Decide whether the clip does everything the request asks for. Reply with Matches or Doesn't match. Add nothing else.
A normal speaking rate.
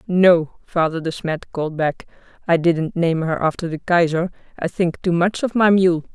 Matches